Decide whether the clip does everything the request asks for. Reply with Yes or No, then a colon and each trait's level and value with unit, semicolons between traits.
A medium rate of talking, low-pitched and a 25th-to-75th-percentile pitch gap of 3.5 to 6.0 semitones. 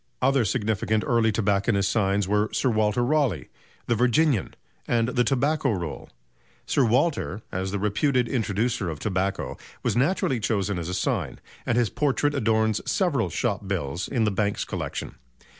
Yes: average, 155 wpm; low, 110 Hz; average, 4.1 semitones